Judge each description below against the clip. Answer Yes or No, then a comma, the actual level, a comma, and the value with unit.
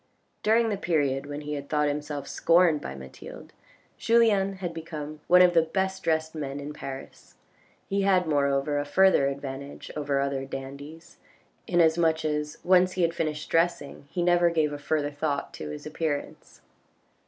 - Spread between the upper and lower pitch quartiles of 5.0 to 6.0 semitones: No, average, 3.4 semitones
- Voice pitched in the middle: Yes, medium, 155 Hz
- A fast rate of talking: No, average, 165 wpm